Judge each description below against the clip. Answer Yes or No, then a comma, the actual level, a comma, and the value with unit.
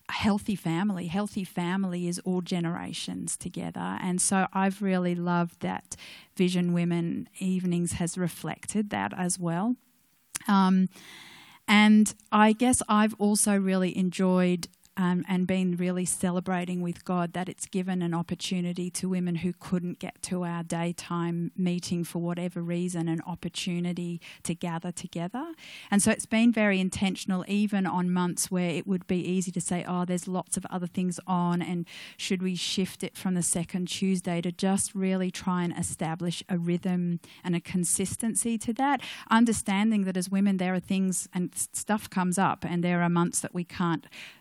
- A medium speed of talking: Yes, average, 165 wpm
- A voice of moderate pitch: Yes, medium, 180 Hz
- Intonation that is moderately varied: No, narrow, 1.8 semitones